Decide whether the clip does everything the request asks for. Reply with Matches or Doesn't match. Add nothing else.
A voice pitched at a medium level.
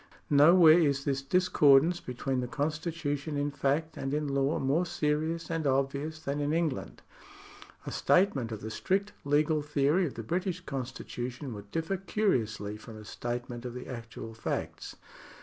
Matches